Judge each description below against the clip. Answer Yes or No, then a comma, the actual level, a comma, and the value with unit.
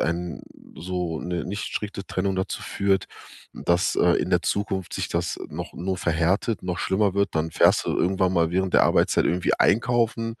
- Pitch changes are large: No, narrow, 2.4 semitones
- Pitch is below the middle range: Yes, very low, 95 Hz